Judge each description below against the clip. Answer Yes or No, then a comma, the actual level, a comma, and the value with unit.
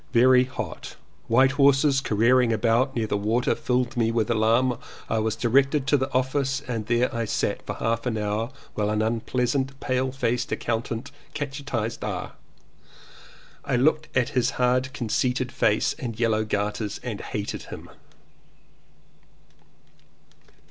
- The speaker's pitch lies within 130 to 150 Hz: No, low, 120 Hz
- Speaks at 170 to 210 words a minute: No, average, 140 wpm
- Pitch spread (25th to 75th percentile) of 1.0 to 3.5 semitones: Yes, average, 2.7 semitones